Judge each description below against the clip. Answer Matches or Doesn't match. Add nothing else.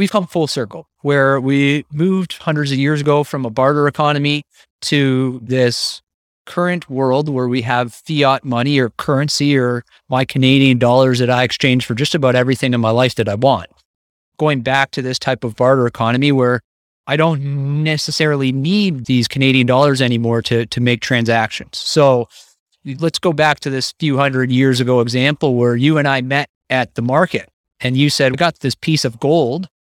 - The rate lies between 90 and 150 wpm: Doesn't match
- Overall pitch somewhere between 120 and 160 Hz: Matches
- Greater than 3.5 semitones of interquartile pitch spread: Doesn't match